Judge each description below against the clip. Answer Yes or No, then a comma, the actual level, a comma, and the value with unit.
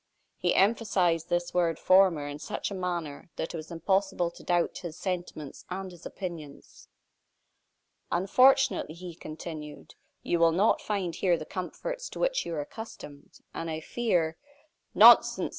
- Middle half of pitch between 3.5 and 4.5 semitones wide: No, average, 3.0 semitones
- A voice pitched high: No, medium, 175 Hz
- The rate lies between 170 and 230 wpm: No, average, 155 wpm